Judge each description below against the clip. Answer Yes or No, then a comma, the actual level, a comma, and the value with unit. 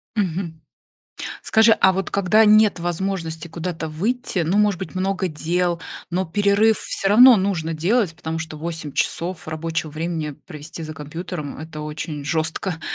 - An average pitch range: Yes, average, 3.5 semitones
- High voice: No, medium, 170 Hz